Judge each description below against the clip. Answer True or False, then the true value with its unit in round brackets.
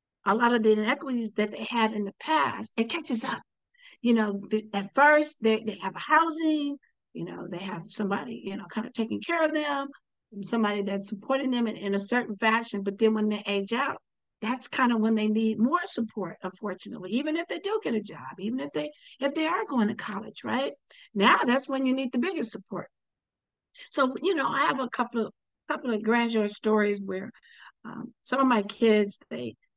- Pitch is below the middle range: False (225 Hz)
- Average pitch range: True (4.2 semitones)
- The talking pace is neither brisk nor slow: False (210 wpm)